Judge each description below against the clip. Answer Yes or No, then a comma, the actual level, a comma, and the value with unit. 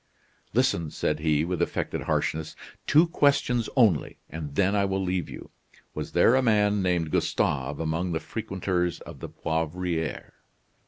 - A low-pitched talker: Yes, very low, 90 Hz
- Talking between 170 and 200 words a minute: No, average, 150 wpm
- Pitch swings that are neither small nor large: Yes, average, 4.3 semitones